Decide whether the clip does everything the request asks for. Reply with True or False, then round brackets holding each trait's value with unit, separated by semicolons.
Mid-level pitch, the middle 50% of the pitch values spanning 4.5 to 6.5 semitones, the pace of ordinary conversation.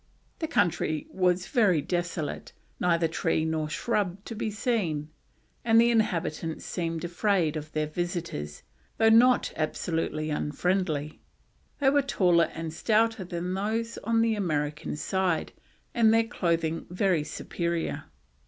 False (175 Hz; 5.3 semitones; 130 wpm)